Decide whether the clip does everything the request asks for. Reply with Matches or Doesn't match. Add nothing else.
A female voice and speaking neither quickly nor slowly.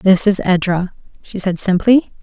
Matches